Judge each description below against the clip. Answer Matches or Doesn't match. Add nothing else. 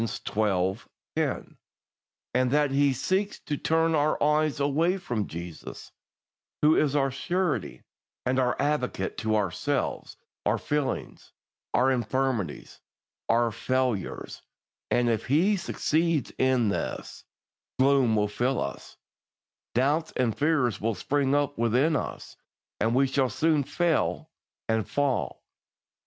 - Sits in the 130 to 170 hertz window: Matches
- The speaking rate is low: Matches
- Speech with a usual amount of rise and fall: Matches